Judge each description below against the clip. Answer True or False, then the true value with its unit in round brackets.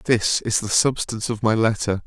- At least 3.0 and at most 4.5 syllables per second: False (5.4 syllables/s)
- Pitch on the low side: True (110 Hz)